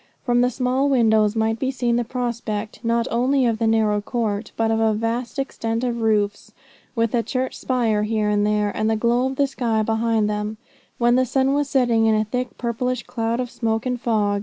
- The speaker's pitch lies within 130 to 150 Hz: No, high, 230 Hz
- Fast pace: Yes, fast, 210 wpm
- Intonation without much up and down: Yes, narrow, 2.3 semitones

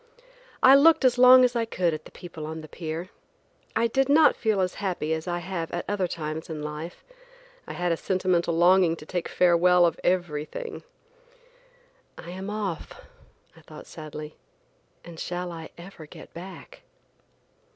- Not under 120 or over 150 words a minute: No, average, 165 wpm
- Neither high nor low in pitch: Yes, medium, 175 Hz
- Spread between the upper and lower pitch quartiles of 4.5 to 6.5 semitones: No, average, 3.4 semitones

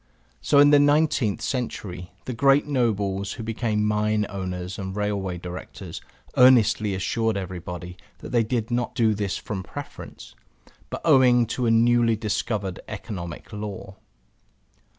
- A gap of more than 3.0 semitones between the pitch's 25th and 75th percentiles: Yes, average, 4.0 semitones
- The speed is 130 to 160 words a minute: Yes, slow, 135 wpm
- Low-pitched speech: Yes, low, 105 Hz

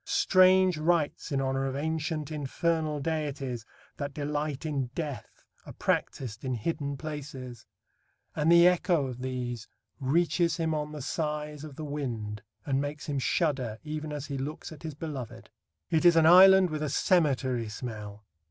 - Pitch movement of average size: Yes, average, 3.3 semitones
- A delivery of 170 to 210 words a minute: No, average, 160 wpm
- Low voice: No, medium, 150 Hz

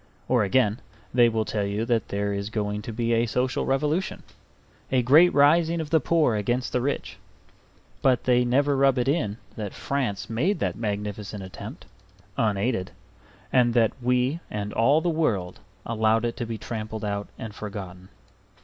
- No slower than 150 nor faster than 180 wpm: Yes, average, 165 wpm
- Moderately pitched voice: No, low, 115 Hz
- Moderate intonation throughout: Yes, average, 4.1 semitones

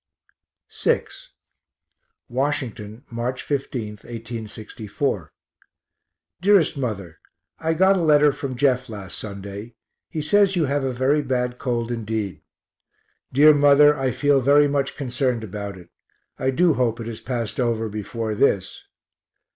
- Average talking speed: No, slow, 130 wpm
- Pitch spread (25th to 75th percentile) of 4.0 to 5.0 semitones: Yes, average, 4.6 semitones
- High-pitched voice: No, low, 125 Hz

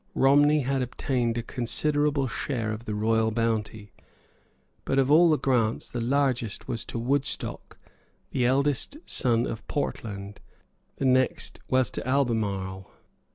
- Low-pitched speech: Yes, low, 125 Hz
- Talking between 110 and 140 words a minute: Yes, slow, 135 wpm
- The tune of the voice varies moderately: Yes, average, 3.6 semitones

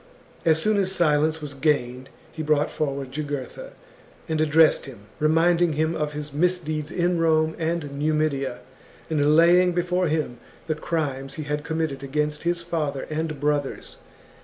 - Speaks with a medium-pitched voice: Yes, medium, 155 Hz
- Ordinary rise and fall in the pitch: No, narrow, 2.2 semitones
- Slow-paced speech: No, average, 150 wpm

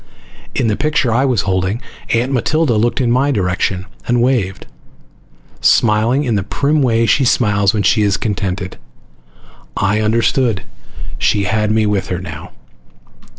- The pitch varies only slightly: No, average, 3.8 semitones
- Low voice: Yes, low, 110 Hz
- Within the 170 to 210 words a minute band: No, average, 150 wpm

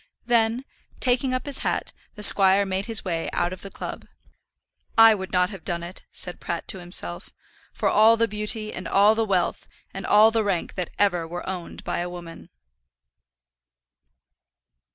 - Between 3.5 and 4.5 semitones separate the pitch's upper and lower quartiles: Yes, average, 3.8 semitones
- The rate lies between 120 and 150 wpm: No, average, 175 wpm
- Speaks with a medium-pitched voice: No, high, 195 Hz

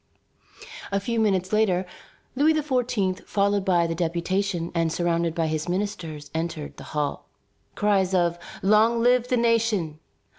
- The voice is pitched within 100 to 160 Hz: No, medium, 185 Hz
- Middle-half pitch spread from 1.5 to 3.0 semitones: No, average, 4.5 semitones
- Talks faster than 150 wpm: No, average, 140 wpm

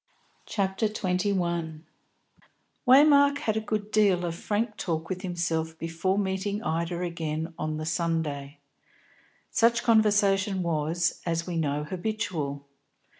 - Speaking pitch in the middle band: Yes, medium, 180 Hz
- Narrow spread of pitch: No, average, 4.2 semitones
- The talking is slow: Yes, slow, 125 wpm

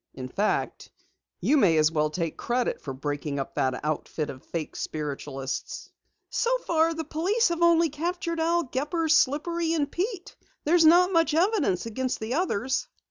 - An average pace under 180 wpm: Yes, average, 160 wpm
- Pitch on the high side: Yes, very high, 295 Hz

